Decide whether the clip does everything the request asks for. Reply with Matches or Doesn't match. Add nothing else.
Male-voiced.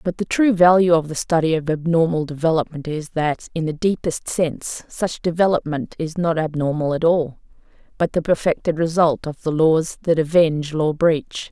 Doesn't match